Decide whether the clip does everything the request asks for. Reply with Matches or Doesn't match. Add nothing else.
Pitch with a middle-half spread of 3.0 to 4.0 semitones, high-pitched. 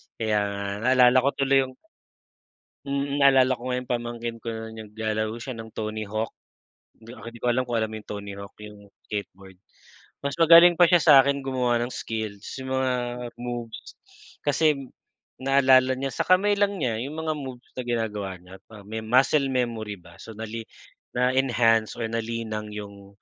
Doesn't match